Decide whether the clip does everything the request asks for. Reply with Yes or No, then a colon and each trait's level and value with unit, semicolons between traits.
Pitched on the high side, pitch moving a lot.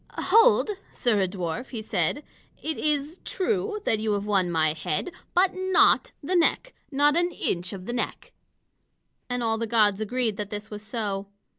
Yes: high, 225 Hz; wide, 7.9 semitones